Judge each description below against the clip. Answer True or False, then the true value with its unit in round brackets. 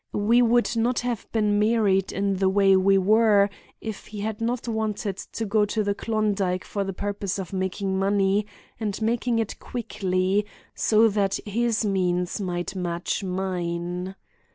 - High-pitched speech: True (200 Hz)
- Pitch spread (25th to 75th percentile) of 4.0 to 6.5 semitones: False (2.4 semitones)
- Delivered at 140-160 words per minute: True (155 wpm)